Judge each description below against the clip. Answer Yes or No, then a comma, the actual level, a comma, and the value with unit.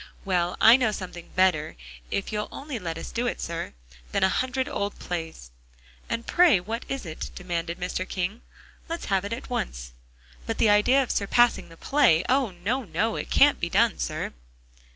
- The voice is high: Yes, high, 200 Hz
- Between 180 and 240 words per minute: Yes, average, 185 wpm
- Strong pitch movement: Yes, wide, 5.8 semitones